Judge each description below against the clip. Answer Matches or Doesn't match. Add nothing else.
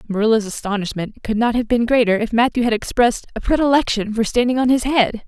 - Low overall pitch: Doesn't match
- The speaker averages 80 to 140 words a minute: Doesn't match